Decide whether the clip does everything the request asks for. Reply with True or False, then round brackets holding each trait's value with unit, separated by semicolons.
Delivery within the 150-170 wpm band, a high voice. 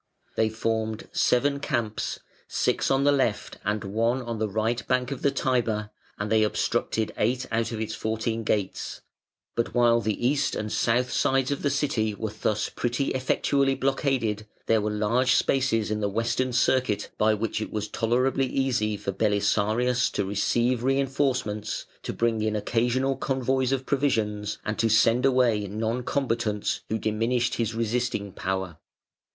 False (160 wpm; 115 Hz)